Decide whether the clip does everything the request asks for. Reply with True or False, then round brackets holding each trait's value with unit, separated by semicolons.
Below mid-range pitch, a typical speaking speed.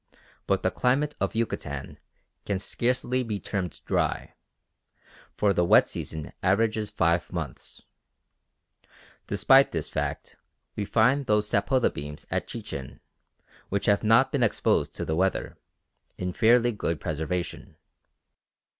False (100 Hz; 125 wpm)